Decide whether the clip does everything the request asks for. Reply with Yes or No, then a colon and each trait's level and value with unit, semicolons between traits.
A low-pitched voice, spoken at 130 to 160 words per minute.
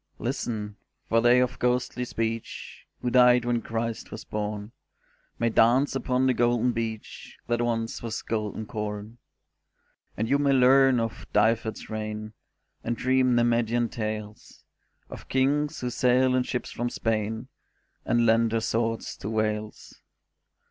Yes: low, 115 Hz; average, 140 wpm